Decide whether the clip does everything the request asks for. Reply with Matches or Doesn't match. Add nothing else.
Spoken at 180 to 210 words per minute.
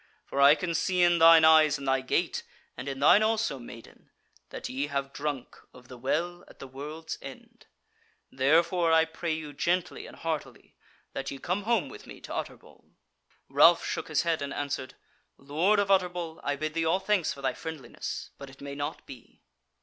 Matches